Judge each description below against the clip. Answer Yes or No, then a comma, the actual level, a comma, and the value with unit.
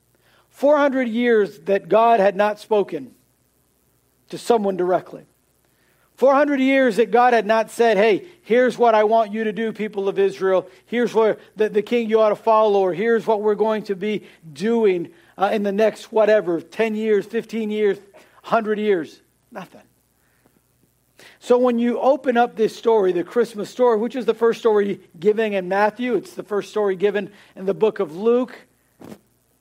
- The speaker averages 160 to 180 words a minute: Yes, average, 170 wpm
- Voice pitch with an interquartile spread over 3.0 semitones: No, narrow, 2.6 semitones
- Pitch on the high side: Yes, high, 215 Hz